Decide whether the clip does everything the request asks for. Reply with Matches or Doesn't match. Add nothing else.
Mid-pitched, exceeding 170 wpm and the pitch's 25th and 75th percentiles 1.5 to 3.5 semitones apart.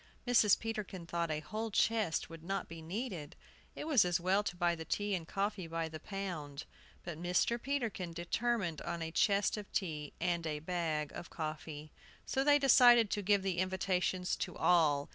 Doesn't match